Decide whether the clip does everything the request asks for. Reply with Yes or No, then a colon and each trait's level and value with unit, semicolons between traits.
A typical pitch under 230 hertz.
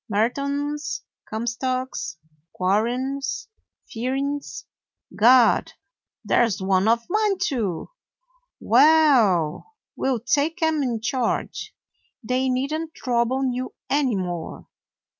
No: very high, 255 Hz